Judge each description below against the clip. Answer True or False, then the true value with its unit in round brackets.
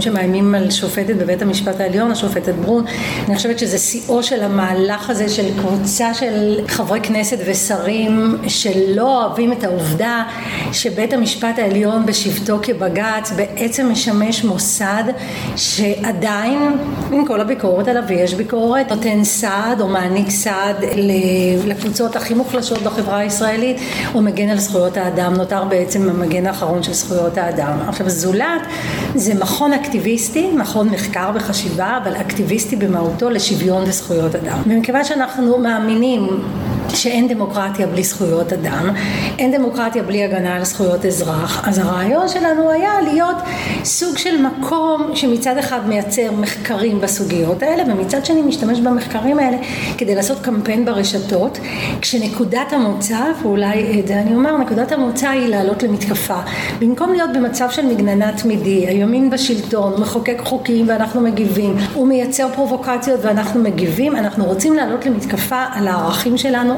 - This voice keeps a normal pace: True (135 wpm)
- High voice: True (215 Hz)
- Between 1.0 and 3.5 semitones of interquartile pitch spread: False (3.9 semitones)